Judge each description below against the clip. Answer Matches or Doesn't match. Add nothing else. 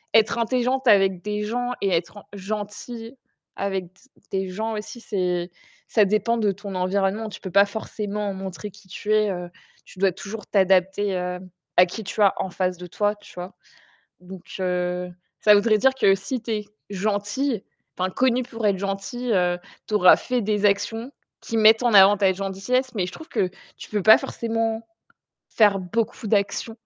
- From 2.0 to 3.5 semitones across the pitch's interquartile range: Matches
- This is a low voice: Doesn't match